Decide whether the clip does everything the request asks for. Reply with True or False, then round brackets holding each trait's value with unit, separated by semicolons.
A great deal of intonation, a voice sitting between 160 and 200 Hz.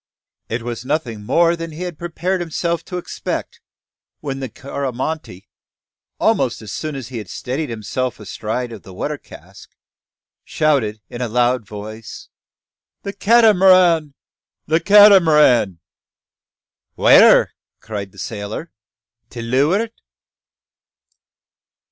False (6.9 semitones; 135 Hz)